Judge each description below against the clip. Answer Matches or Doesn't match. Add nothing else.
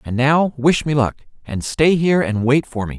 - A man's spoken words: Matches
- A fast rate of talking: Matches